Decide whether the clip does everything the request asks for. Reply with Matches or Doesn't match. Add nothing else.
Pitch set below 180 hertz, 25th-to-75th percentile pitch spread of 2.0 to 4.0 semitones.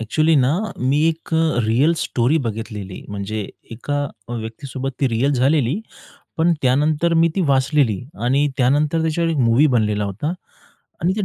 Doesn't match